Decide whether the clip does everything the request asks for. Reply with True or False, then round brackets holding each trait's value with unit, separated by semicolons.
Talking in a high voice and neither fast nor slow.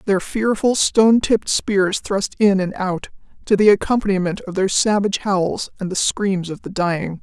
True (195 Hz; 185 wpm)